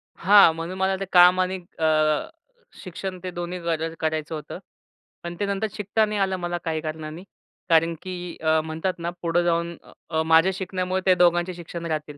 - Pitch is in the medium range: Yes, medium, 175 Hz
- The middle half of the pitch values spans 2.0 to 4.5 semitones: Yes, narrow, 2.4 semitones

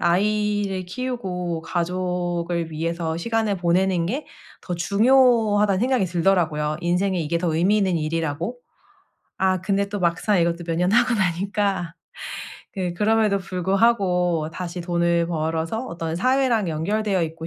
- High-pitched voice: No, medium, 180 Hz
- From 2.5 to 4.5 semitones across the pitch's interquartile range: Yes, average, 3.3 semitones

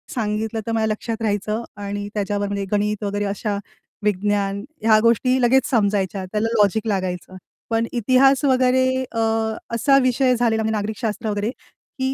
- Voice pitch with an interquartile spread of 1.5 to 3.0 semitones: Yes, narrow, 2.6 semitones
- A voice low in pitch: No, high, 215 Hz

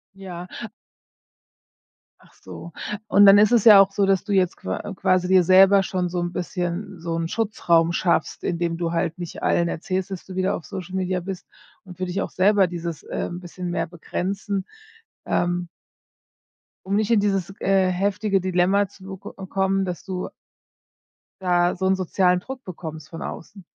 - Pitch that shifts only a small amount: Yes, narrow, 1.9 semitones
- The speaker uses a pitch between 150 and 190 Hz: Yes, medium, 185 Hz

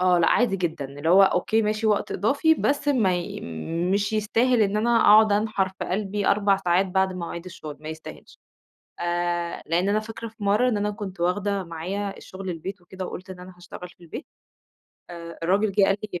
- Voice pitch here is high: Yes, high, 195 Hz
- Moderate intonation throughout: Yes, average, 3.2 semitones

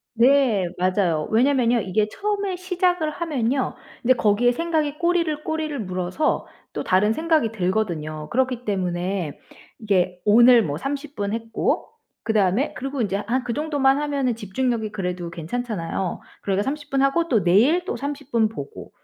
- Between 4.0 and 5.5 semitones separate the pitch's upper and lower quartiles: No, wide, 6.8 semitones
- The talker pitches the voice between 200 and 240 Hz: Yes, high, 235 Hz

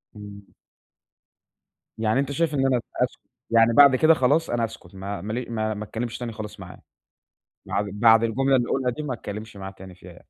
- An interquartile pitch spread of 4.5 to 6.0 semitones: No, average, 3.9 semitones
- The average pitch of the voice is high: No, low, 115 Hz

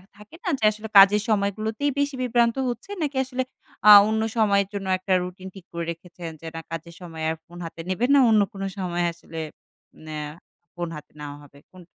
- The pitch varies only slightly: No, average, 4.5 semitones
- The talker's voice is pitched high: Yes, high, 195 Hz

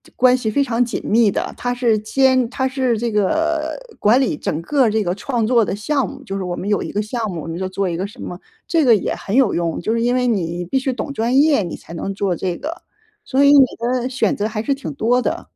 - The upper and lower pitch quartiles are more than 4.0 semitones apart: Yes, average, 4.9 semitones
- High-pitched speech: Yes, high, 230 Hz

